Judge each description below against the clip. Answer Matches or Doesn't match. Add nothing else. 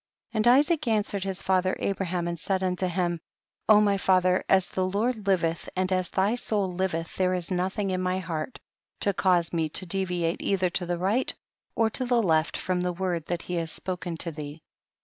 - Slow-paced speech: Doesn't match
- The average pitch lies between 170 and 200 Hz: Matches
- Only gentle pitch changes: Matches